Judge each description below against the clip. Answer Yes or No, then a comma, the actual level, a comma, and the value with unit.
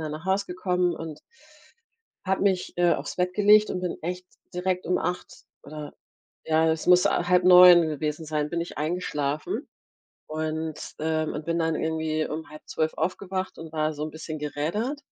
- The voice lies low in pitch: No, medium, 165 Hz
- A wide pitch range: No, narrow, 2.6 semitones